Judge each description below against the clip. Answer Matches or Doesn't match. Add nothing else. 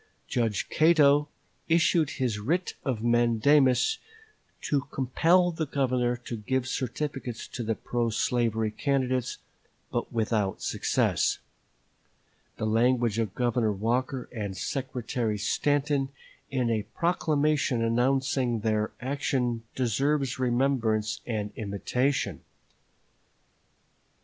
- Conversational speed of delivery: Doesn't match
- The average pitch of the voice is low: Matches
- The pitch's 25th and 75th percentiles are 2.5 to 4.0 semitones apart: Matches